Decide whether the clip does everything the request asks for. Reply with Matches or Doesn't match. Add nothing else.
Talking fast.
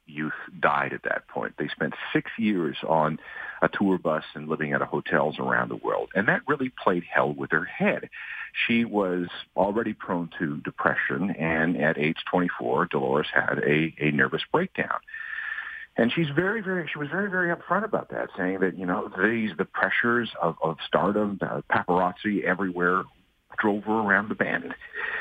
Doesn't match